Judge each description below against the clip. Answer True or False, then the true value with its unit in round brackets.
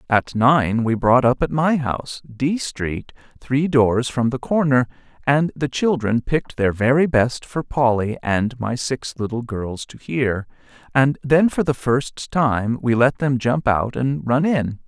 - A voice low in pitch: True (130 Hz)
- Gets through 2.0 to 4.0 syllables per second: True (3.9 syllables/s)